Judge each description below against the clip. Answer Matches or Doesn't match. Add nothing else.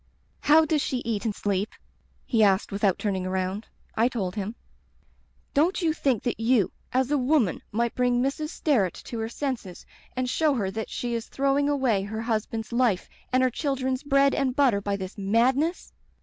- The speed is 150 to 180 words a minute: Doesn't match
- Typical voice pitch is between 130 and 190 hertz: Doesn't match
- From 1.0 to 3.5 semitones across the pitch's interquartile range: Doesn't match